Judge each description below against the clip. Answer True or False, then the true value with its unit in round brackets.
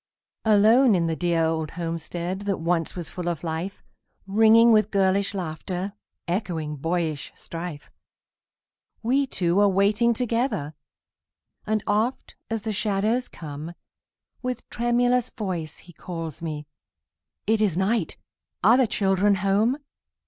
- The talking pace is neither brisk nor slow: False (125 wpm)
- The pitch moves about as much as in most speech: True (4.6 semitones)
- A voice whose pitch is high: True (195 Hz)